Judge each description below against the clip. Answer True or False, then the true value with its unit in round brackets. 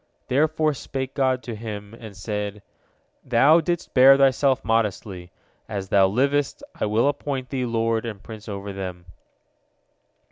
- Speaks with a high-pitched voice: False (115 Hz)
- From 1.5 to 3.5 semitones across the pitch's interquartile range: False (4.8 semitones)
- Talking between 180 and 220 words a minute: False (140 wpm)